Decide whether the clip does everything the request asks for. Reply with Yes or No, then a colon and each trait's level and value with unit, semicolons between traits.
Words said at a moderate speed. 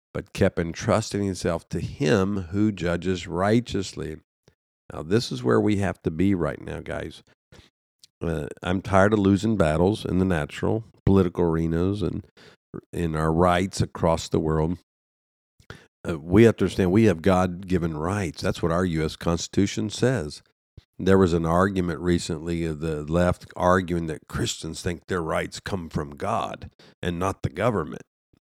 Yes: average, 160 wpm